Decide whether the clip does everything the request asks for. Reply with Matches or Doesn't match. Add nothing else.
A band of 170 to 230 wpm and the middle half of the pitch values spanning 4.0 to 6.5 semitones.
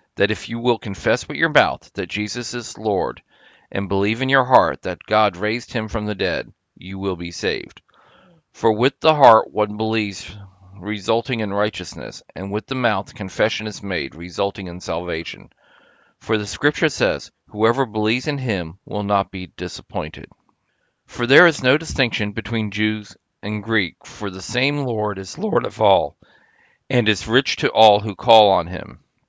Doesn't match